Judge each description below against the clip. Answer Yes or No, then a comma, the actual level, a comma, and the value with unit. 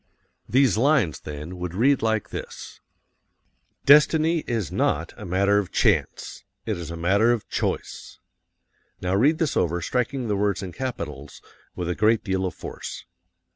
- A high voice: No, low, 100 Hz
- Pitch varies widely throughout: Yes, wide, 5.9 semitones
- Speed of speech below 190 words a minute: Yes, average, 155 wpm